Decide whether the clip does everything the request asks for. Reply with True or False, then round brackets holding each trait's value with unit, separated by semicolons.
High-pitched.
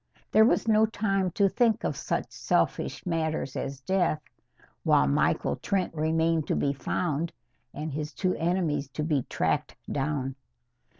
False (160 Hz)